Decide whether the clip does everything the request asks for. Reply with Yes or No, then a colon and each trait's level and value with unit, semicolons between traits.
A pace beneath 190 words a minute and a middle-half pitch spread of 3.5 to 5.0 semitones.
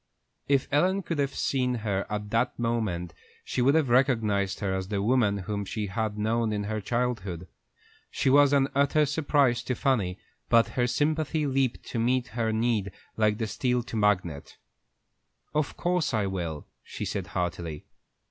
Yes: average, 170 wpm; average, 4.7 semitones